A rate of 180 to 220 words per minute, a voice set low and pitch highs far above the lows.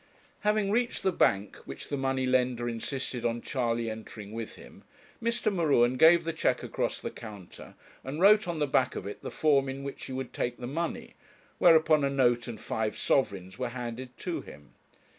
No: average, 190 wpm; low, 130 Hz; average, 5.0 semitones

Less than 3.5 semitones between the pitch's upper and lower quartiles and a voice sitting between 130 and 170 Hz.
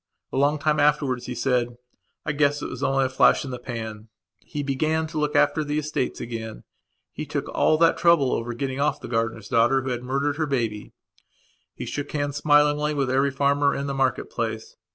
Yes: average, 3.1 semitones; medium, 140 Hz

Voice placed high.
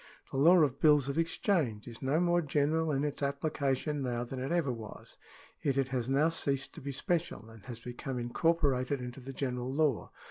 No: medium, 140 Hz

